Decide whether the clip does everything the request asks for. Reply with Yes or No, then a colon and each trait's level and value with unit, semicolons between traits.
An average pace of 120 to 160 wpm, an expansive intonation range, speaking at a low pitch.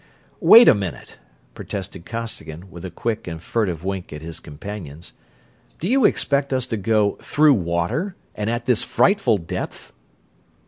Yes: average, 150 wpm; wide, 6.4 semitones; low, 105 Hz